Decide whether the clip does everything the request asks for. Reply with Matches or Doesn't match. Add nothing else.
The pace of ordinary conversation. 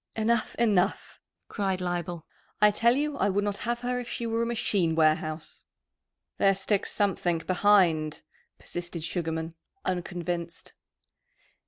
Doesn't match